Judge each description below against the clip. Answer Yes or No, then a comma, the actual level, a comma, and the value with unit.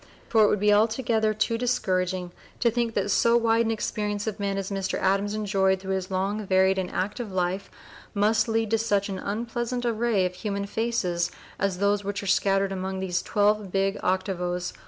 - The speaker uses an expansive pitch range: No, narrow, 2.6 semitones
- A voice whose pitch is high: Yes, high, 200 Hz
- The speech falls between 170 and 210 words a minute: Yes, average, 200 wpm